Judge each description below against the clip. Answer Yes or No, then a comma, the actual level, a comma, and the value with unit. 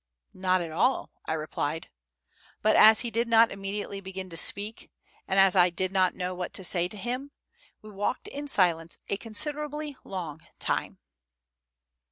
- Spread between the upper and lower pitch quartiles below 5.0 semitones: Yes, average, 4.0 semitones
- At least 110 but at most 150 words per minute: No, average, 165 wpm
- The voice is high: Yes, high, 195 Hz